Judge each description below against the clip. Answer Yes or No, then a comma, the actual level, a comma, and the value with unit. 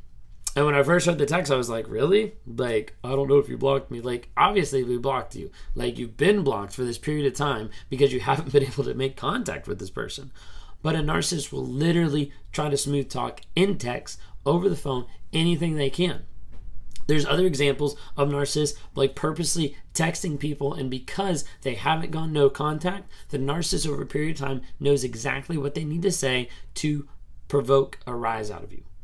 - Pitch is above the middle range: No, medium, 140 Hz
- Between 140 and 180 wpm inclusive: No, average, 200 wpm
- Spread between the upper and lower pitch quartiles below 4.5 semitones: Yes, average, 3.6 semitones